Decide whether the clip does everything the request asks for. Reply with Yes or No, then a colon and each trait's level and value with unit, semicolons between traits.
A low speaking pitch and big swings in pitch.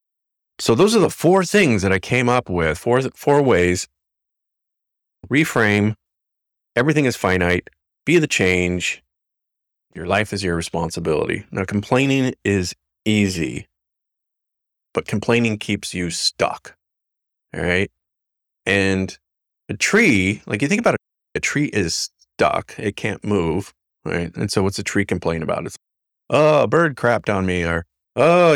Yes: low, 100 Hz; wide, 5.7 semitones